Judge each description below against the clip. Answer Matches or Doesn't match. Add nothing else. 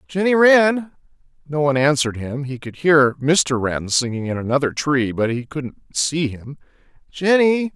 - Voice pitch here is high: Doesn't match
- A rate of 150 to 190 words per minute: Matches